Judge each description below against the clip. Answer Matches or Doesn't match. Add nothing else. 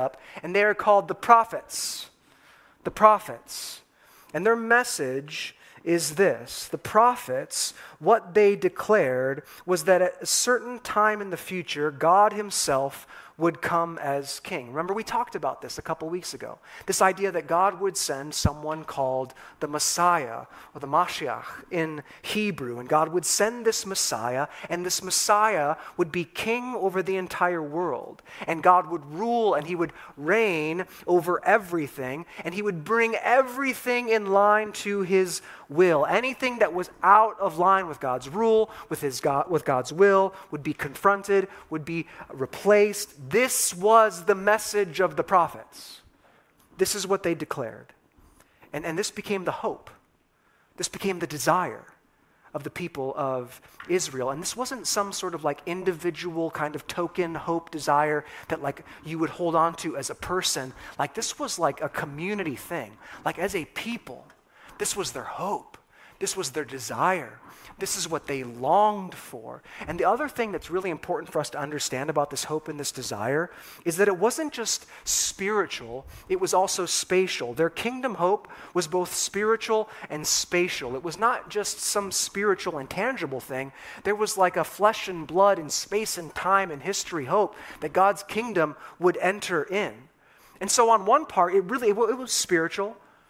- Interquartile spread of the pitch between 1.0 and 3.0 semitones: Doesn't match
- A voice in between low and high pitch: Matches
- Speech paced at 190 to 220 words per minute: Doesn't match